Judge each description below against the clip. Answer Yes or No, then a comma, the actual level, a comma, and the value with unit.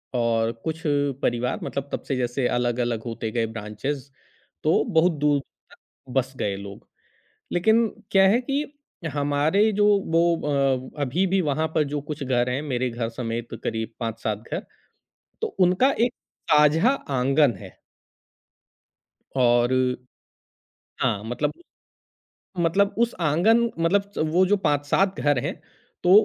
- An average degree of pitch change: No, wide, 6.5 semitones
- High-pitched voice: No, medium, 145 Hz